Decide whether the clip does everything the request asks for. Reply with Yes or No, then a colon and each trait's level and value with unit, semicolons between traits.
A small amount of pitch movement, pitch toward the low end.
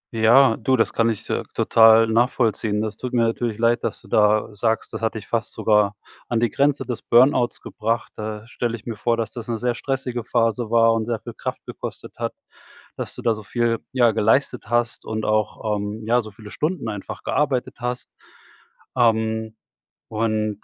Yes: narrow, 1.7 semitones; low, 115 Hz